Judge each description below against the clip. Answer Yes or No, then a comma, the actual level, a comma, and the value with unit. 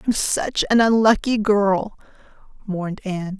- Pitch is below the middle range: No, high, 205 Hz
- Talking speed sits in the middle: No, slow, 125 wpm